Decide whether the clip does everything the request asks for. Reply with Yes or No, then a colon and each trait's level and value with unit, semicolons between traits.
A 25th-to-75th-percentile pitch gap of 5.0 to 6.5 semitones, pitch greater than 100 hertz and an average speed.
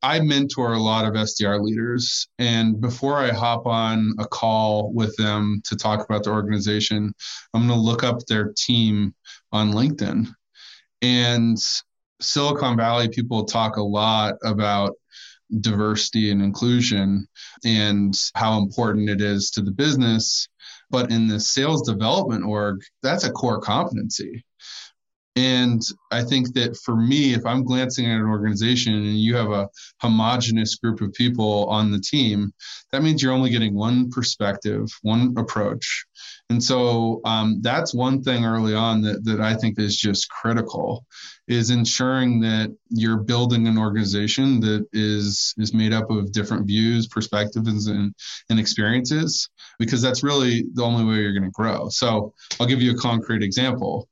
No: narrow, 2.4 semitones; low, 110 Hz; average, 155 wpm